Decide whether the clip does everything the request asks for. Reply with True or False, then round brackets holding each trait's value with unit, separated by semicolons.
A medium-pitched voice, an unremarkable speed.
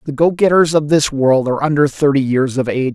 False (145 Hz; 245 wpm)